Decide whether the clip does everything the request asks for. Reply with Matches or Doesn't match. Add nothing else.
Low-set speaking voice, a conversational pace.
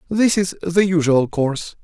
Doesn't match